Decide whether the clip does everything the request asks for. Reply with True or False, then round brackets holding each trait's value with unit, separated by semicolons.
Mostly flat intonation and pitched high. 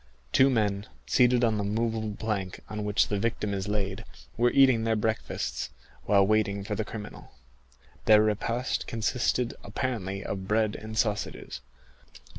False (1.9 semitones; 110 Hz)